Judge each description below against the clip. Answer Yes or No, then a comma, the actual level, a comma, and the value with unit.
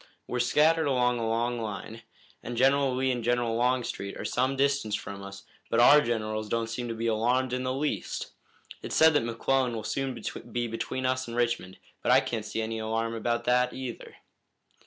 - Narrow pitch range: Yes, narrow, 2.3 semitones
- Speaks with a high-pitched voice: No, low, 120 Hz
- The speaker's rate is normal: Yes, average, 195 wpm